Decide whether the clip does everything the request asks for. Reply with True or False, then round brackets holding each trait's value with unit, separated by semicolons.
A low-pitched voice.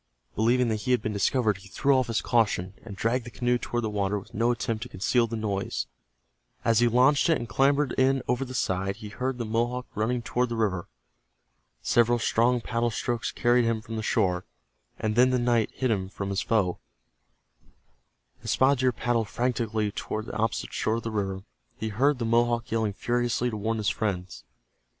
True (115 Hz)